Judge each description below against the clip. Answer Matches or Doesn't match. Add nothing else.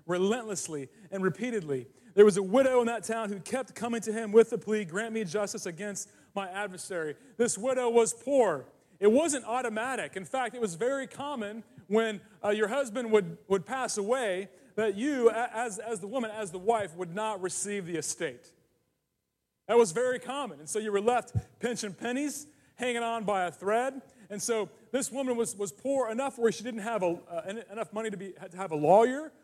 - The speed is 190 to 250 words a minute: Matches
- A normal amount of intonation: Matches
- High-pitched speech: Matches